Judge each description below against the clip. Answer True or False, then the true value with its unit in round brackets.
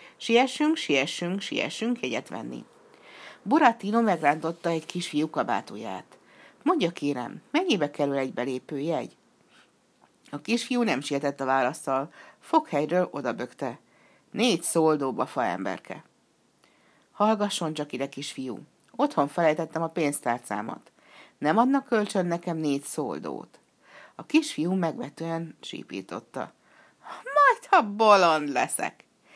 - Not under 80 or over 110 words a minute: True (105 wpm)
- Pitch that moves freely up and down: True (7.5 semitones)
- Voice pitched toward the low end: False (165 Hz)